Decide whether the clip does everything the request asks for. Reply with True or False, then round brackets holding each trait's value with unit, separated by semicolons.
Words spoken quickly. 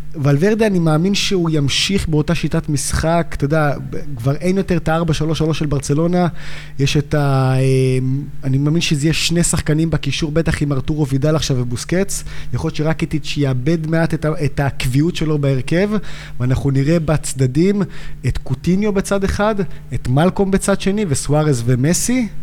True (155 wpm)